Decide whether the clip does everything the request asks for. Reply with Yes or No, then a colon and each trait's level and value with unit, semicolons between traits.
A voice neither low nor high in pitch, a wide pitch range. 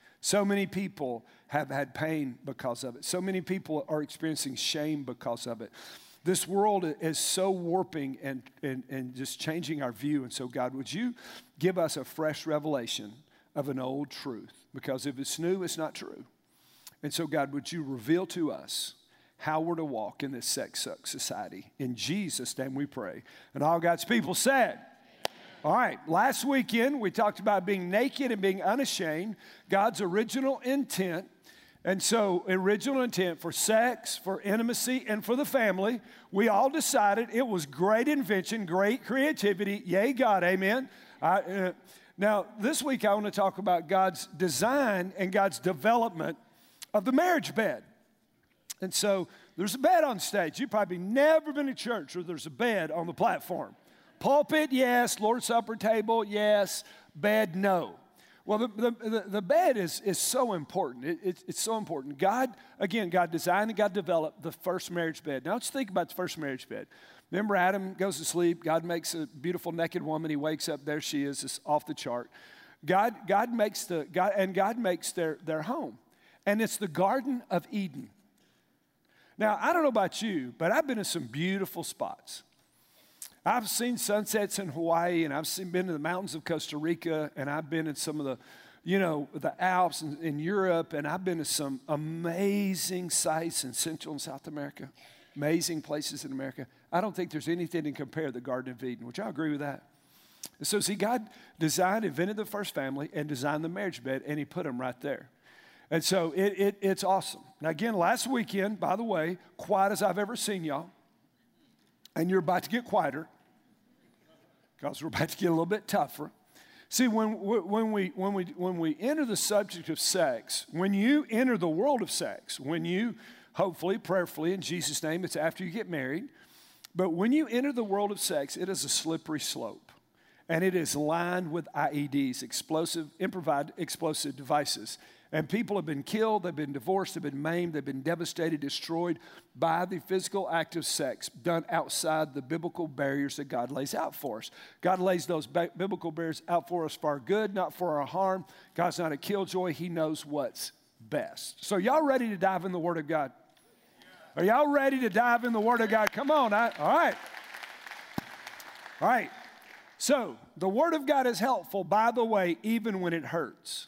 No: medium, 180 Hz; average, 4.8 semitones